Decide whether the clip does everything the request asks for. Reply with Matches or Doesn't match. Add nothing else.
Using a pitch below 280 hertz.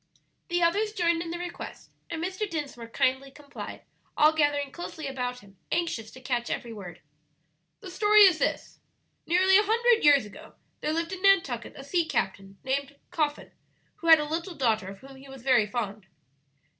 Doesn't match